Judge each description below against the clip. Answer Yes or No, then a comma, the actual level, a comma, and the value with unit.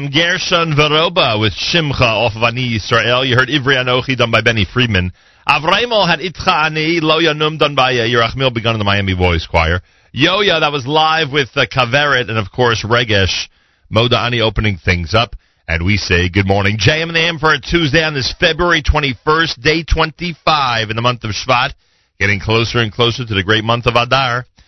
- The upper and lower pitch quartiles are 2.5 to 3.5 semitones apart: No, wide, 5.6 semitones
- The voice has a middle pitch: No, low, 120 Hz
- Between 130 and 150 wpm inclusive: No, average, 185 wpm